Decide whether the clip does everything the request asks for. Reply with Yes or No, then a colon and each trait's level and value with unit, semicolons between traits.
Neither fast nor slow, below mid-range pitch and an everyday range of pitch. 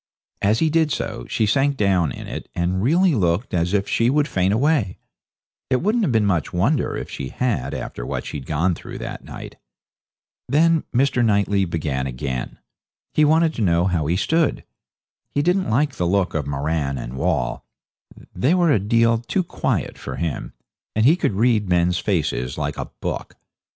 No: average, 180 wpm; low, 100 Hz; wide, 8.7 semitones